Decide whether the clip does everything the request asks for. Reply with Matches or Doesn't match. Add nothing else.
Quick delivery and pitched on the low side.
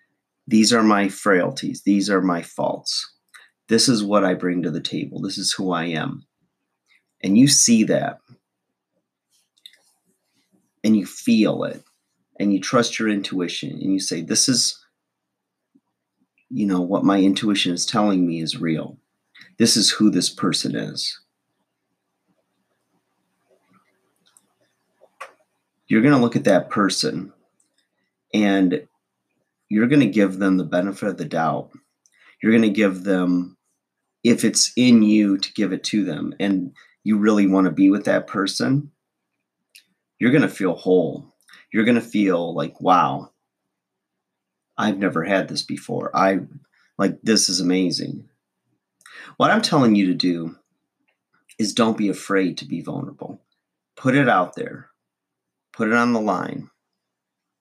Doesn't match